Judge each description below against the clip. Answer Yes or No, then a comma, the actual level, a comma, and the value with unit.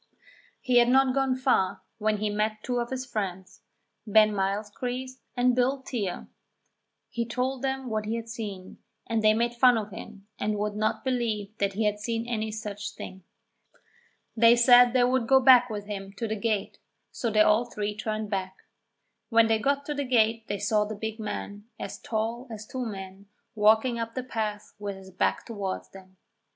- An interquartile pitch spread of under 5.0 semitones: Yes, average, 2.9 semitones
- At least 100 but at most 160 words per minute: No, average, 190 wpm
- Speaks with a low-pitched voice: No, high, 220 Hz